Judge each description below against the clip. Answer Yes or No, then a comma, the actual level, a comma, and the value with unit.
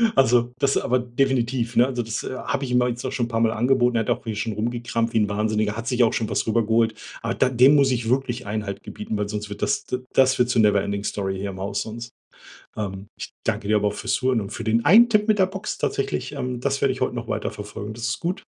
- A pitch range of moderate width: Yes, average, 3.1 semitones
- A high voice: No, low, 115 Hz